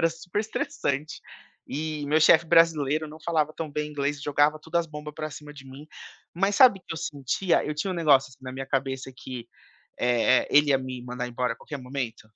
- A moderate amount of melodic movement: Yes, average, 3.1 semitones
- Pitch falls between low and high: Yes, medium, 150 Hz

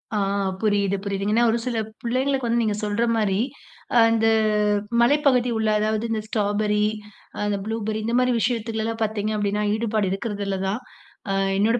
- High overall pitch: Yes, high, 220 Hz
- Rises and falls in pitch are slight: Yes, narrow, 2.0 semitones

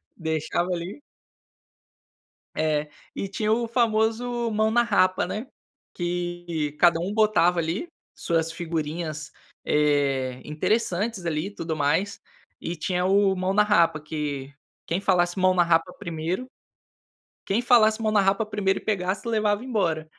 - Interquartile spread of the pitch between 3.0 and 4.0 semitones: No, average, 4.7 semitones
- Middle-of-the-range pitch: Yes, medium, 180 Hz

